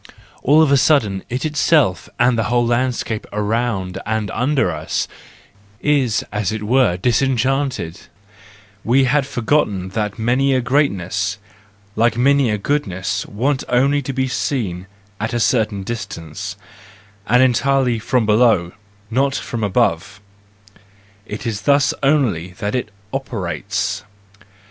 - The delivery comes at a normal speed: No, slow, 130 wpm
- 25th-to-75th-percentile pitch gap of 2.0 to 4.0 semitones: No, average, 4.8 semitones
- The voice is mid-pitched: No, low, 115 Hz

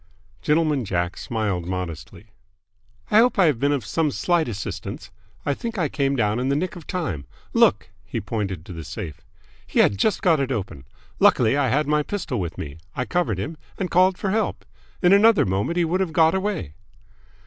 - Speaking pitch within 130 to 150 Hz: Yes, medium, 140 Hz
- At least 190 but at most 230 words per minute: Yes, average, 195 wpm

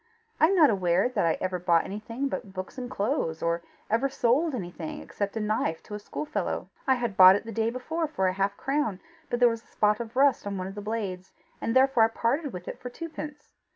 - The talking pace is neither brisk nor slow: No, fast, 235 wpm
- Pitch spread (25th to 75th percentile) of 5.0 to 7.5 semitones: Yes, wide, 5.5 semitones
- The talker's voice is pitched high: Yes, high, 225 Hz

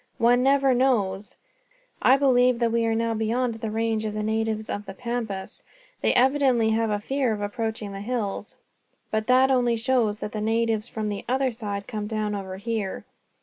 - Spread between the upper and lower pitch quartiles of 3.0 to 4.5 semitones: No, narrow, 2.6 semitones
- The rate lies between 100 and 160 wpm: No, average, 190 wpm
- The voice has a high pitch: Yes, high, 225 Hz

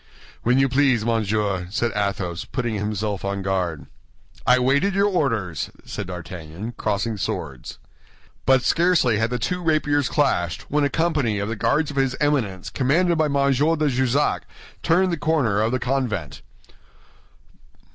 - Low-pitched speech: Yes, low, 125 Hz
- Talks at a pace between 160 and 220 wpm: No, average, 150 wpm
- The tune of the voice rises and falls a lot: Yes, wide, 6.2 semitones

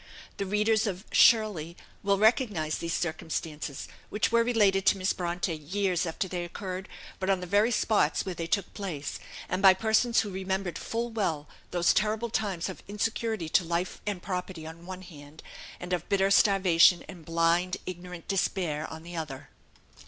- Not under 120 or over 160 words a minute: No, average, 175 wpm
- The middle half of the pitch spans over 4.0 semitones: No, average, 3.3 semitones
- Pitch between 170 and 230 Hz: Yes, medium, 185 Hz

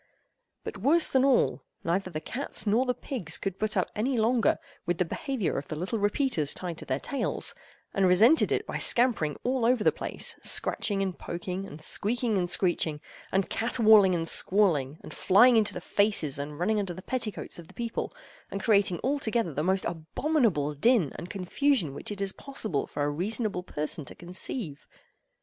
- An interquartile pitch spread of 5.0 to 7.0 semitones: Yes, wide, 5.6 semitones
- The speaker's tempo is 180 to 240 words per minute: Yes, average, 185 wpm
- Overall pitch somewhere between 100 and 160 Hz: No, high, 195 Hz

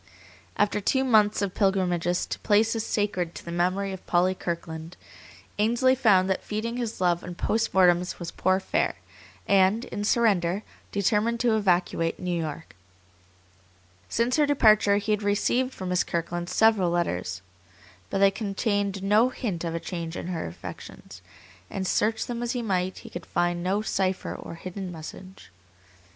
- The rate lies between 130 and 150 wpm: No, average, 160 wpm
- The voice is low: No, high, 195 Hz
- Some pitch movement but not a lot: Yes, average, 3.6 semitones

